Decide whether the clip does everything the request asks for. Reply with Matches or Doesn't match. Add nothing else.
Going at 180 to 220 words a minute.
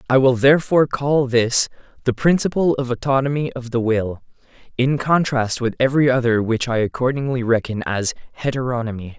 Doesn't match